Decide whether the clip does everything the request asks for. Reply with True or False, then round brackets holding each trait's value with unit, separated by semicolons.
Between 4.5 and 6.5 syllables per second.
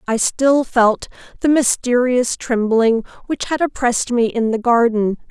False (4.3 syllables/s)